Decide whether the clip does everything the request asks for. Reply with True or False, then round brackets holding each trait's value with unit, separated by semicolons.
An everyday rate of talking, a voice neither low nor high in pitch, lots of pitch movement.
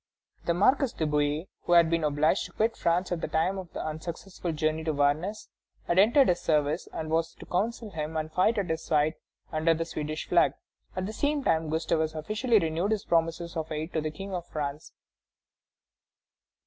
False (195 wpm; 165 Hz; 3.1 semitones)